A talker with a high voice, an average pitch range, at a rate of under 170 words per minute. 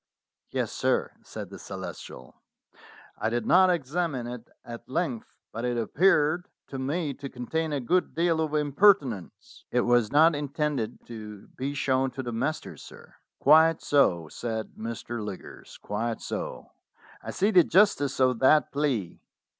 No: low, 135 Hz; average, 5.0 semitones; average, 150 wpm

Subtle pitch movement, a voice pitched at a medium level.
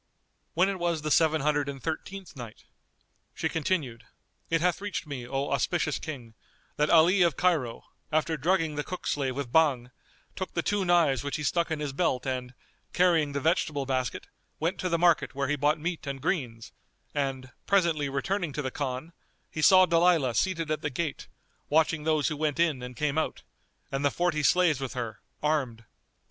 No: average, 3.7 semitones; medium, 150 Hz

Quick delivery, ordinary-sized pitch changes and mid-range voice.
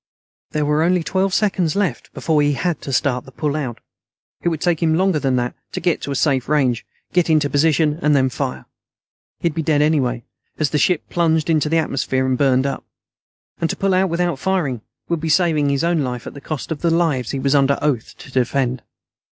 Yes: fast, 215 wpm; average, 3.7 semitones; medium, 150 Hz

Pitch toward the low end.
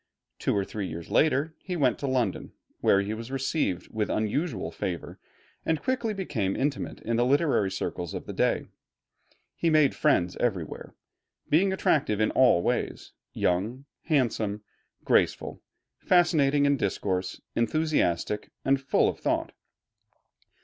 Yes: low, 125 Hz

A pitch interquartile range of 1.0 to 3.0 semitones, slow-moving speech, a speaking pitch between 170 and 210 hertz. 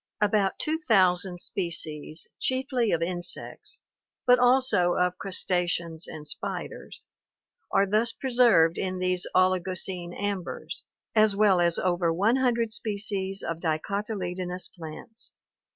No: average, 3.7 semitones; slow, 115 wpm; medium, 185 Hz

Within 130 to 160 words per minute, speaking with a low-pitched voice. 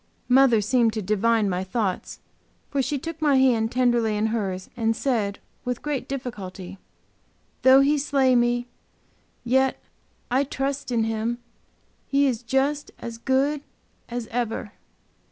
No: average, 140 wpm; high, 240 Hz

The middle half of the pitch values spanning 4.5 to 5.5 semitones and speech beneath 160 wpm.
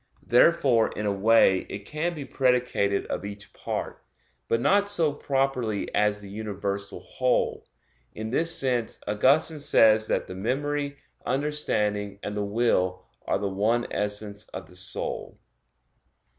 Yes: average, 5.0 semitones; average, 140 wpm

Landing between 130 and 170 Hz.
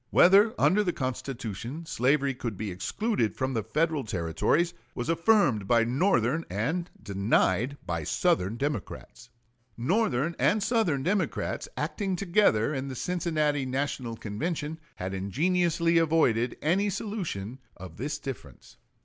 Yes: medium, 140 Hz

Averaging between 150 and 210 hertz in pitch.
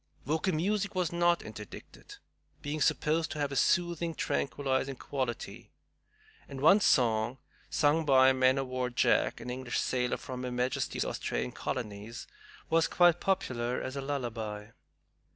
No: low, 135 Hz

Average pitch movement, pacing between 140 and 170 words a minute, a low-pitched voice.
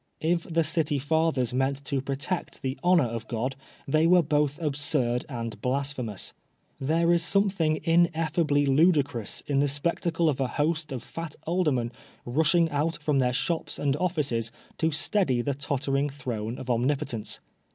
No: average, 3.9 semitones; average, 150 wpm; medium, 145 Hz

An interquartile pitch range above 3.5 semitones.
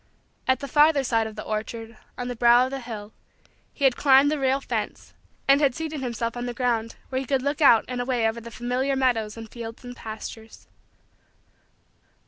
No: average, 2.9 semitones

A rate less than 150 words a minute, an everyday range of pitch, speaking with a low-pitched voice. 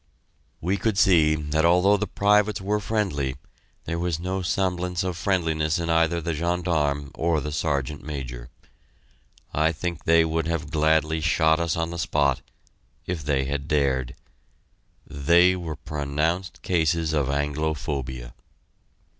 Yes: average, 140 wpm; average, 3.0 semitones; very low, 80 Hz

